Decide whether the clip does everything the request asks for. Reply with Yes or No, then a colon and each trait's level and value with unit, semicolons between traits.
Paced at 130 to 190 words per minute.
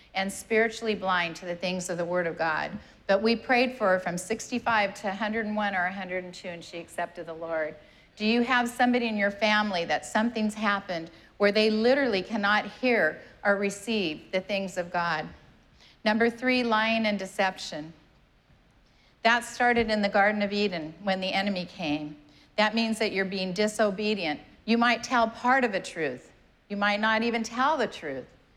Yes: average, 175 wpm